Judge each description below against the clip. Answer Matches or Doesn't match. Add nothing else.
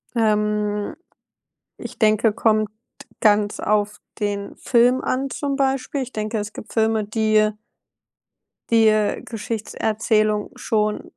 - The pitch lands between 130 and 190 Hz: Doesn't match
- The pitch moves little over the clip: Matches